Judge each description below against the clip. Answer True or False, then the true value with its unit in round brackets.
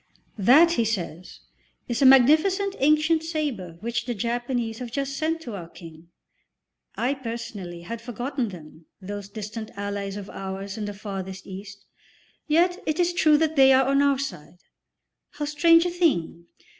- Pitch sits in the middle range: False (235 Hz)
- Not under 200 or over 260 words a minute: False (160 wpm)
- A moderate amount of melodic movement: False (7.1 semitones)